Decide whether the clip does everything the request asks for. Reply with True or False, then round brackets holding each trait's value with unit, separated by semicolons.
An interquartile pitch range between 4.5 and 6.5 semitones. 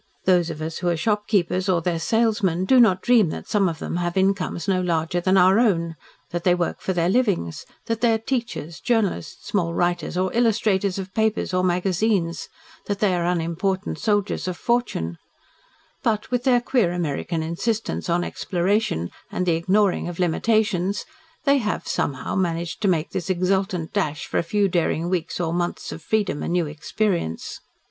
False (3.6 semitones)